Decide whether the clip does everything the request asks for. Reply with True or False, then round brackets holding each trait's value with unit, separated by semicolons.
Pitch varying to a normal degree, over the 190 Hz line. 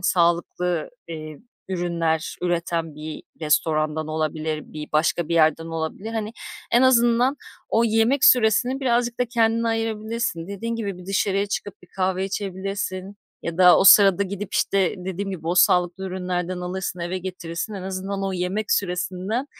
False (3.9 semitones; 185 Hz)